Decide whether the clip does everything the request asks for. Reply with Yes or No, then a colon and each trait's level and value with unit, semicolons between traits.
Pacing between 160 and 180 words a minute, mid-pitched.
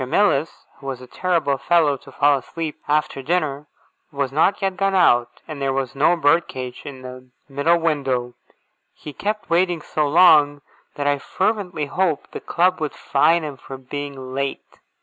Yes: average, 175 wpm; medium, 145 Hz